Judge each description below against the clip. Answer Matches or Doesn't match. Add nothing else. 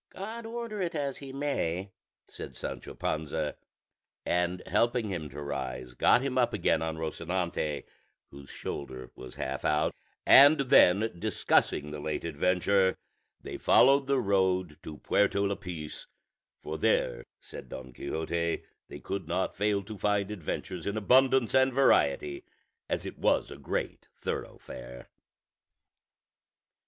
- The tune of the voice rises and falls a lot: Matches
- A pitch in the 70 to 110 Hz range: Matches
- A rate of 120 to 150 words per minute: Matches